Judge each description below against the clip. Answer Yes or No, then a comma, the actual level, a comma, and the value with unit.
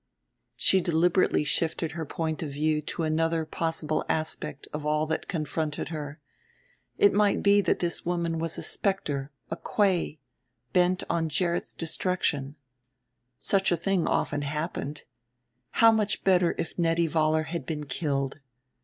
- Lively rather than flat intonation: No, narrow, 2.6 semitones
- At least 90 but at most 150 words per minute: Yes, average, 145 wpm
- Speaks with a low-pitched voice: No, medium, 165 Hz